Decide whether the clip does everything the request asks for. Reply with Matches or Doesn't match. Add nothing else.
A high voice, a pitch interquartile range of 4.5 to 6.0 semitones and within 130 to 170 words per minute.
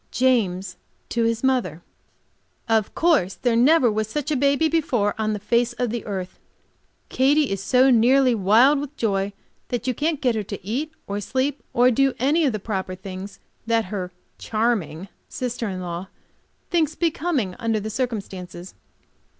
Matches